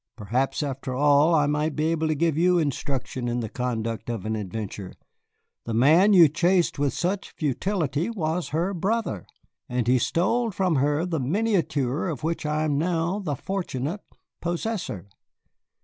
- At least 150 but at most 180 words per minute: Yes, average, 160 wpm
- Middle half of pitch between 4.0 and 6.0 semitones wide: Yes, wide, 5.4 semitones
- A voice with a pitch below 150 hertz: No, medium, 155 Hz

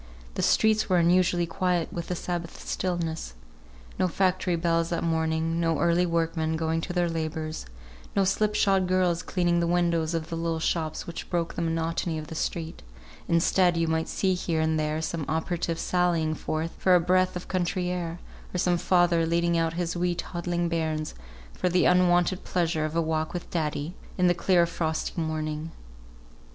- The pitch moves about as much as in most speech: No, narrow, 1.6 semitones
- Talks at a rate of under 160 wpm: No, average, 180 wpm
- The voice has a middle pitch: Yes, medium, 170 Hz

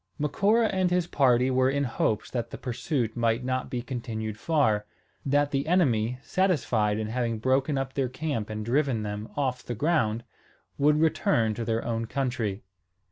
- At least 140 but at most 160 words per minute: No, average, 170 wpm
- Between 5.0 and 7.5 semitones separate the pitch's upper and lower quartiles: No, average, 4.2 semitones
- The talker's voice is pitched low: Yes, low, 125 Hz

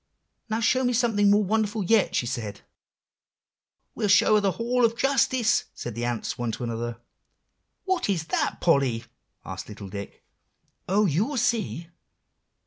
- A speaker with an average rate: Yes, average, 150 wpm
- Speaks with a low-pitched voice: No, high, 205 Hz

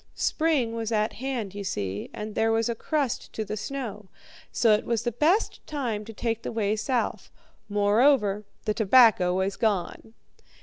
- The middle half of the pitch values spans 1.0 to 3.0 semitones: Yes, narrow, 2.6 semitones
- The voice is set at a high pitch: Yes, high, 220 Hz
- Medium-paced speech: Yes, average, 170 wpm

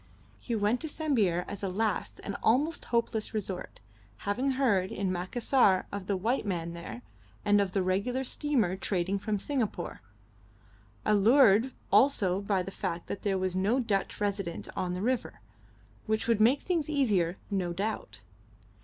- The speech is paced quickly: No, average, 155 wpm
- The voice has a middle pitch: No, high, 205 Hz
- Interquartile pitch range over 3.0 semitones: Yes, average, 4.5 semitones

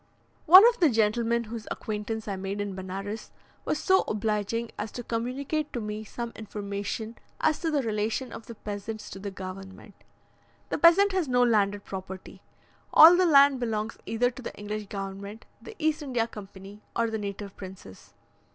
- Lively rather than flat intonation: No, average, 3.4 semitones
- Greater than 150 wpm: Yes, average, 170 wpm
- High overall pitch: Yes, high, 220 Hz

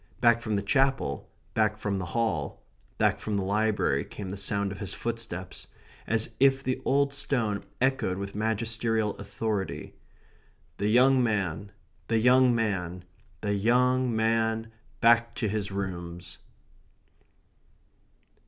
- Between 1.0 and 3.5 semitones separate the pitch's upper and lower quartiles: Yes, average, 3.0 semitones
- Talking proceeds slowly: Yes, slow, 130 wpm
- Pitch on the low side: Yes, low, 110 Hz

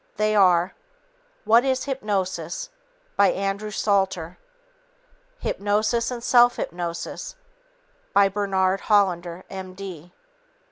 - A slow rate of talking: Yes, slow, 90 wpm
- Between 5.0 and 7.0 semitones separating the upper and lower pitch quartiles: No, average, 2.7 semitones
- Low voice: No, high, 195 Hz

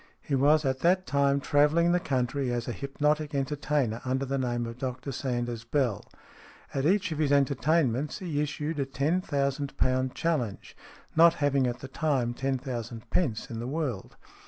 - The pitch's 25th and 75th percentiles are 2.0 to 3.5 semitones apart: Yes, average, 3.1 semitones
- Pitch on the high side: No, medium, 140 Hz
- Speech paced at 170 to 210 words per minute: Yes, average, 175 wpm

